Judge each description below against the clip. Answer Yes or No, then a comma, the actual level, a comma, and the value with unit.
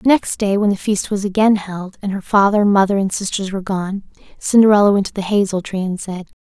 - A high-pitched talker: Yes, high, 200 Hz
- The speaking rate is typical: No, fast, 235 wpm